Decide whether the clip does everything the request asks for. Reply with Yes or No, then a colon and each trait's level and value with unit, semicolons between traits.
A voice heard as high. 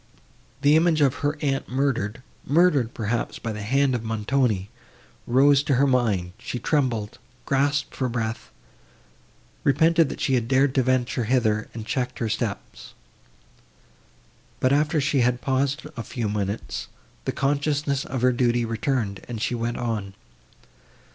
No: low, 125 Hz